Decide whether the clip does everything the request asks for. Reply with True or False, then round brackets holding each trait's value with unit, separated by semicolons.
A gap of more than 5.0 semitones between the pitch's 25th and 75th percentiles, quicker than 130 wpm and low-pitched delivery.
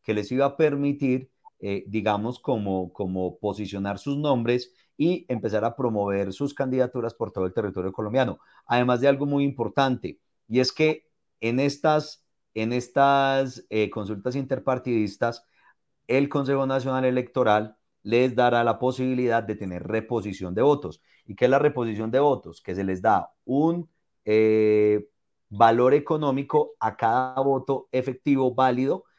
False (4.2 semitones; 145 wpm; 125 Hz)